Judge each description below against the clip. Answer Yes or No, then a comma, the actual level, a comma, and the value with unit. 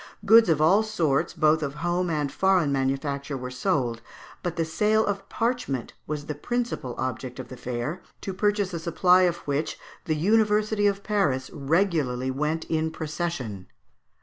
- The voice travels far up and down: Yes, wide, 6.0 semitones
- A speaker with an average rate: Yes, average, 160 wpm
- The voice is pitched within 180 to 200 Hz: No, medium, 160 Hz